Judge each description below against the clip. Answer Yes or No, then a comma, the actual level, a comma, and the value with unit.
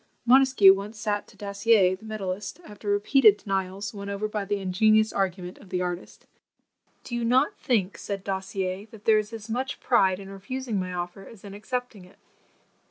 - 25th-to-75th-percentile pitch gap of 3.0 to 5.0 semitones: No, narrow, 2.5 semitones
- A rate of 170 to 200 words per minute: Yes, average, 180 wpm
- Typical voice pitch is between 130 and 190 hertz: No, high, 205 Hz